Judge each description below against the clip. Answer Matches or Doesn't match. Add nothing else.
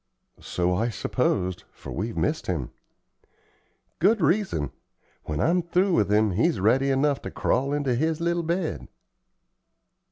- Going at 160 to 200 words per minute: Doesn't match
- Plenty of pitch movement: Matches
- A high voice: Doesn't match